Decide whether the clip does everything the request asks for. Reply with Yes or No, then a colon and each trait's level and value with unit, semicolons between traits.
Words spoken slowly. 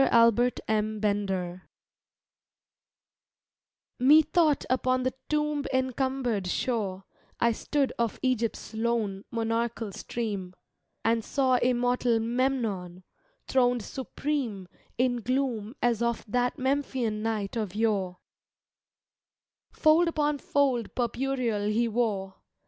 Yes: slow, 100 wpm